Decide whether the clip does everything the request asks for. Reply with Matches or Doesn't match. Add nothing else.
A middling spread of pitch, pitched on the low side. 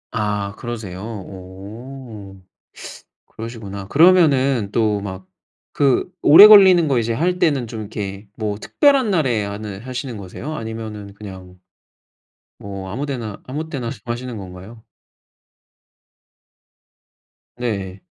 Matches